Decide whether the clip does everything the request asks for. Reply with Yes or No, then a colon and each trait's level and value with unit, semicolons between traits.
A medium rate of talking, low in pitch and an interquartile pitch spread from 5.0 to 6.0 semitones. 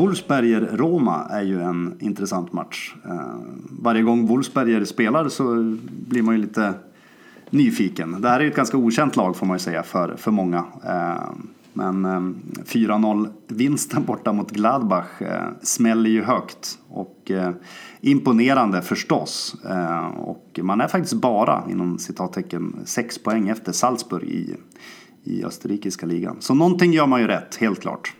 Yes: average, 150 wpm; low, 110 Hz; wide, 5.4 semitones